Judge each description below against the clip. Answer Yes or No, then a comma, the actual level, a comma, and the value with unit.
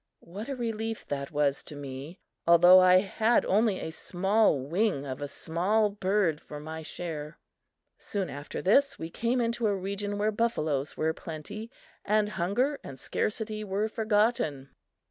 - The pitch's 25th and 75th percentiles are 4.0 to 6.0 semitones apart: Yes, wide, 5.5 semitones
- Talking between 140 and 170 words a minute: Yes, average, 155 wpm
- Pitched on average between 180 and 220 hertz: Yes, high, 190 Hz